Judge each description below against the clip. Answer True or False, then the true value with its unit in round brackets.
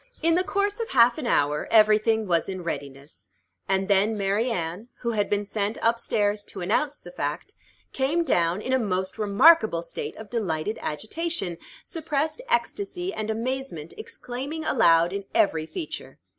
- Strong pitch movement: True (6.5 semitones)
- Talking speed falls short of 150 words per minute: False (165 wpm)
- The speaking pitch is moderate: False (215 Hz)